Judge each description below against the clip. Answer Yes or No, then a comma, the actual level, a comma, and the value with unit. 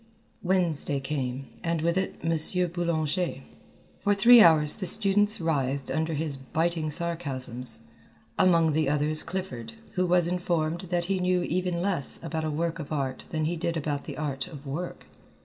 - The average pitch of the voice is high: No, medium, 165 Hz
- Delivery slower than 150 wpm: No, average, 165 wpm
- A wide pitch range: No, average, 3.4 semitones